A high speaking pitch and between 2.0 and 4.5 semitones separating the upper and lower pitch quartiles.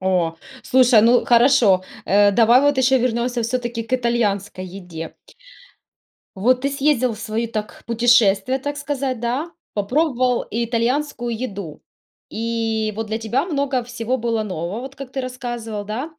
Yes: high, 235 Hz; average, 3.0 semitones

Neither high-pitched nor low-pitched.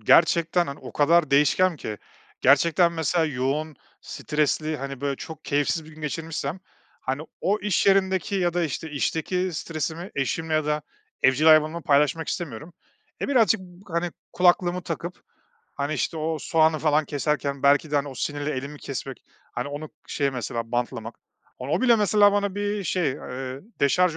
Yes: medium, 155 Hz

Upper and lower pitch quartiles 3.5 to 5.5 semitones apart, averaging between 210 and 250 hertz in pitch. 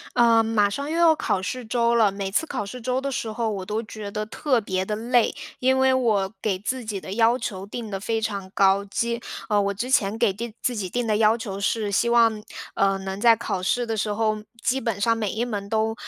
No: average, 2.8 semitones; high, 220 Hz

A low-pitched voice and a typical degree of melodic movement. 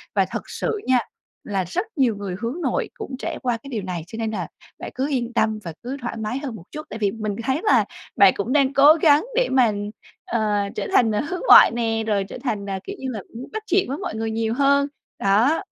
No: high, 235 Hz; average, 4.7 semitones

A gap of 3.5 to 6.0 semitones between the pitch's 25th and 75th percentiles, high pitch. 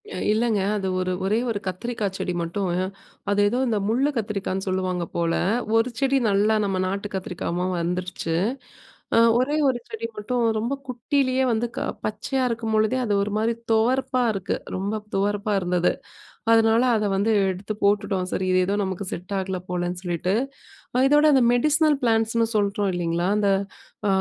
Yes: average, 3.8 semitones; high, 205 Hz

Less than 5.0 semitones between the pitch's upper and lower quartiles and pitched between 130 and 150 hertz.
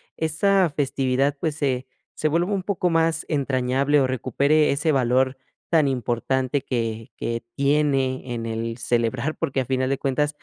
Yes: average, 3.0 semitones; low, 135 Hz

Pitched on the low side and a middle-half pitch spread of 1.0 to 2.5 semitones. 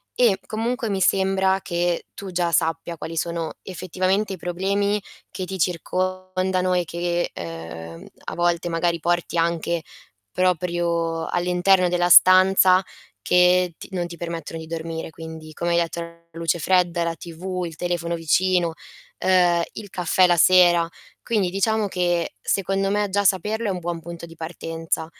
No: medium, 175 Hz; narrow, 1.8 semitones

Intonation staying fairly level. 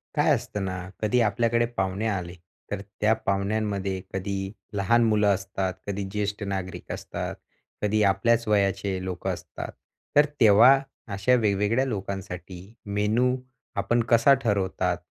Yes: narrow, 2.3 semitones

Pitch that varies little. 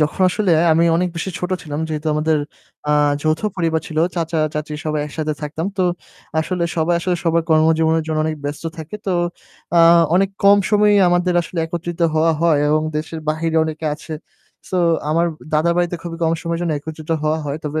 Yes: narrow, 1.8 semitones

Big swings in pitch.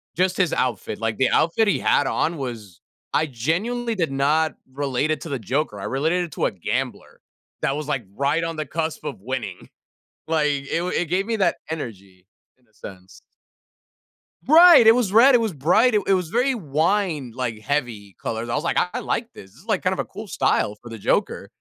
Yes: wide, 7.2 semitones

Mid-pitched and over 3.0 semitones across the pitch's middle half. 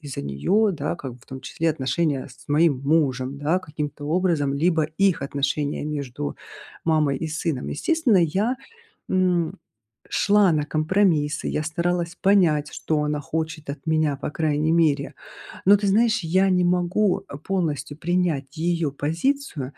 Yes: medium, 160 Hz; average, 3.6 semitones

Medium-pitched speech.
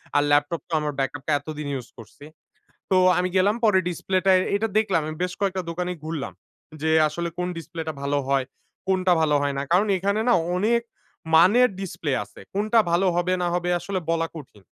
Yes: medium, 175 Hz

